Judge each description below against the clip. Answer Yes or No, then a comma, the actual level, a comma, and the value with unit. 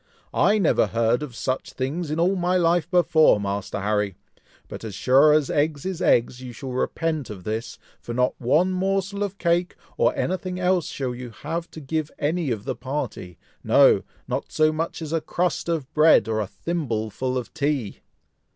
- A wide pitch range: Yes, wide, 5.9 semitones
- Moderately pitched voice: Yes, medium, 150 Hz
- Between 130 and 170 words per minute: No, average, 185 wpm